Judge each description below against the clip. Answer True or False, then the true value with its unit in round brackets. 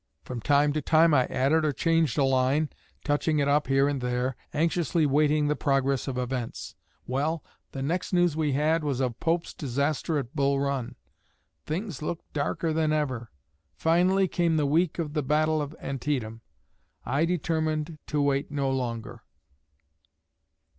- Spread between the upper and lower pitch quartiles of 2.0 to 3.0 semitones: True (2.7 semitones)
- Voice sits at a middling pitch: True (145 Hz)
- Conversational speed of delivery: True (160 wpm)